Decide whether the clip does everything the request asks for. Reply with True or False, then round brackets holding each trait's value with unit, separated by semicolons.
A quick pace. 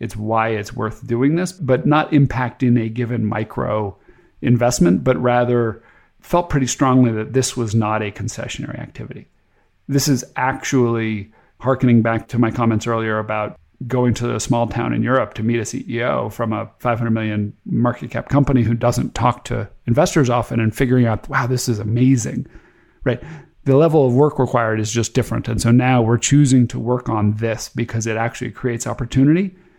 False (180 wpm)